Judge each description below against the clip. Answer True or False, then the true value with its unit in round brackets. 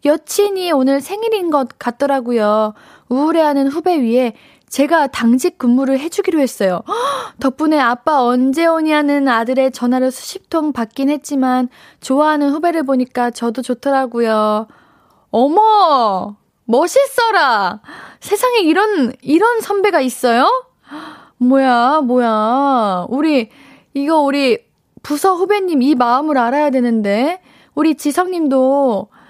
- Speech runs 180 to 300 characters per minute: True (260 characters per minute)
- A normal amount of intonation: True (4.5 semitones)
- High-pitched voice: True (280 Hz)